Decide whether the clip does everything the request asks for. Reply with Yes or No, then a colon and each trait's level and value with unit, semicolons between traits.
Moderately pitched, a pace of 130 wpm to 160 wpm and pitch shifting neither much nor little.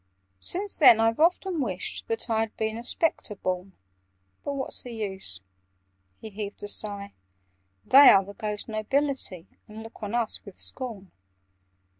No: high, 220 Hz; average, 155 wpm; average, 4.0 semitones